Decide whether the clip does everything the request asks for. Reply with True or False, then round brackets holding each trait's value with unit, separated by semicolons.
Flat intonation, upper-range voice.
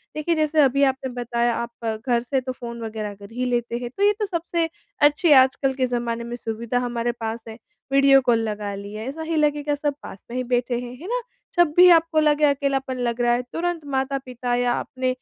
False (3.7 semitones; 255 Hz)